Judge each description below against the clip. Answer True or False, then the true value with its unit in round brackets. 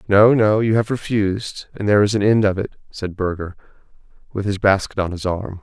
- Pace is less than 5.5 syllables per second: False (5.6 syllables/s)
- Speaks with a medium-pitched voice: False (100 Hz)